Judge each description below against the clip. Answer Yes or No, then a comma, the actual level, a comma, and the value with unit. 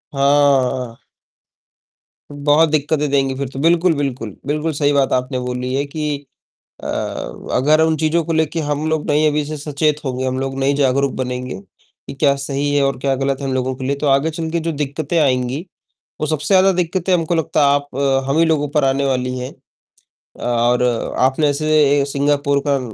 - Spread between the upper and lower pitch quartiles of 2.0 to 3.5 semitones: Yes, narrow, 2.5 semitones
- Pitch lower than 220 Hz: Yes, medium, 140 Hz